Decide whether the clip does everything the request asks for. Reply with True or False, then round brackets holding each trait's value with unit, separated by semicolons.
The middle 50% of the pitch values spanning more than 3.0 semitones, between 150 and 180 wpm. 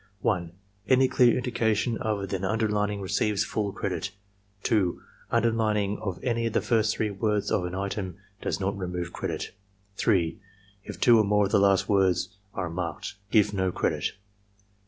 False (2.6 semitones; 165 wpm)